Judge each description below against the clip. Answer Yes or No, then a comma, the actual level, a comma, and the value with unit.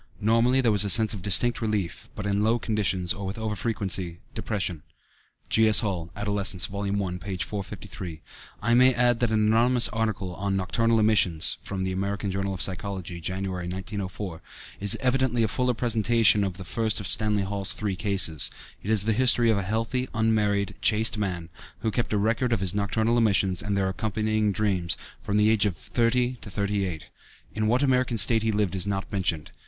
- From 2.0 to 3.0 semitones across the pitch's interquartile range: Yes, average, 2.7 semitones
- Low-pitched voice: Yes, low, 105 Hz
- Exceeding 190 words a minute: No, average, 185 wpm